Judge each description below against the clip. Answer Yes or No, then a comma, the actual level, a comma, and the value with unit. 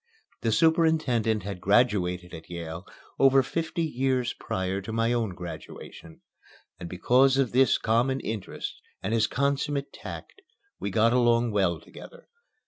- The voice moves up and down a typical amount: No, wide, 5.9 semitones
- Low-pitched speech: Yes, low, 115 Hz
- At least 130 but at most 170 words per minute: Yes, slow, 135 wpm